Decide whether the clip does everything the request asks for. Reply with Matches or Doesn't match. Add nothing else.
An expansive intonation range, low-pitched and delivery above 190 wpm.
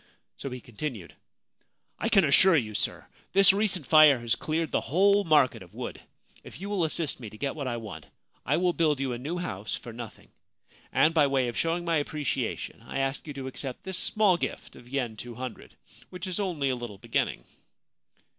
Doesn't match